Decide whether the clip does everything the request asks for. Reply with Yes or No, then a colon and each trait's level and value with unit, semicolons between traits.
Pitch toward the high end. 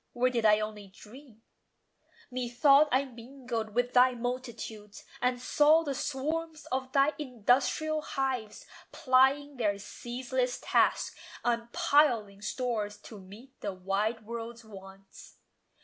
Yes: high, 245 Hz